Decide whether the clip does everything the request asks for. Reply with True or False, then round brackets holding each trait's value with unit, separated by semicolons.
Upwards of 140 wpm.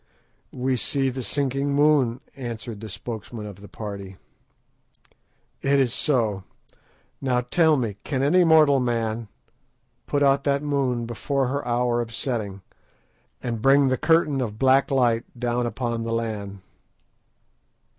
False (135 wpm)